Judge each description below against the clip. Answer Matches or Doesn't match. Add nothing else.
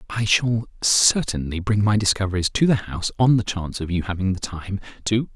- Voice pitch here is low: Matches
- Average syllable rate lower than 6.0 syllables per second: Matches